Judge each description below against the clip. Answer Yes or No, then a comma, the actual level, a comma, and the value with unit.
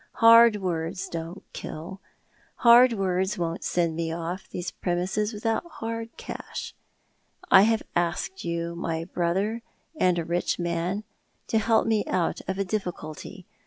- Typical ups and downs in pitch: Yes, average, 4.0 semitones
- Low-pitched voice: No, medium, 185 Hz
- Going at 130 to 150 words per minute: Yes, average, 145 wpm